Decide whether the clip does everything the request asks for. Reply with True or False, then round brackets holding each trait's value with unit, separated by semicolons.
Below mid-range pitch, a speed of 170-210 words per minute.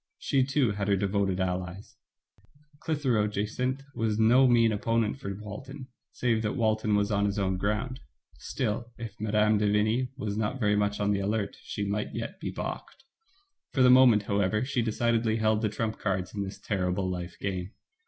True (105 Hz; 180 wpm)